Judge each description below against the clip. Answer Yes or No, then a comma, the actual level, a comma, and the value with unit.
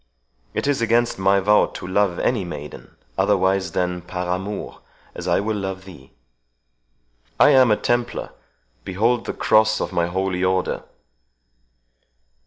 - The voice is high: No, very low, 95 Hz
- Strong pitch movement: No, average, 3.1 semitones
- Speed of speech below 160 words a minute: Yes, average, 140 wpm